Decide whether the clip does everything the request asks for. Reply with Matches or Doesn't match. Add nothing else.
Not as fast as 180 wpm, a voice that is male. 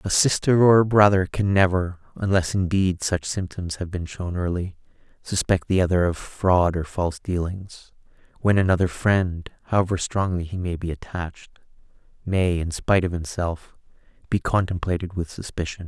Matches